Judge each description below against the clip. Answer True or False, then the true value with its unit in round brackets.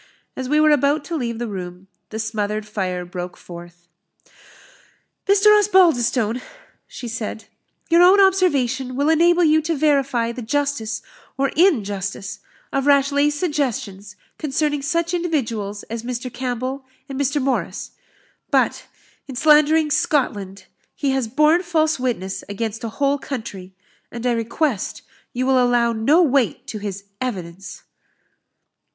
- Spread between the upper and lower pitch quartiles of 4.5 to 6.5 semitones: True (5.4 semitones)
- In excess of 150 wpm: False (135 wpm)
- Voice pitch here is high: True (255 Hz)